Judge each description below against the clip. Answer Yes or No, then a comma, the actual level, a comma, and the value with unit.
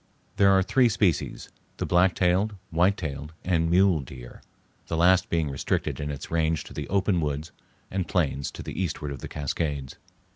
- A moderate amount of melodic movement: Yes, average, 4.2 semitones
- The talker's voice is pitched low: Yes, very low, 85 Hz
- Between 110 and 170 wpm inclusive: No, average, 180 wpm